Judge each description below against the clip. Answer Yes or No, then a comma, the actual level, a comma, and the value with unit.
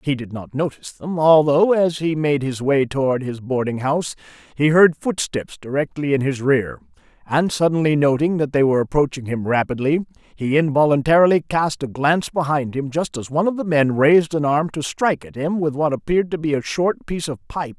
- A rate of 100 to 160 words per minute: No, fast, 205 wpm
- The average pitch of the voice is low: No, medium, 145 Hz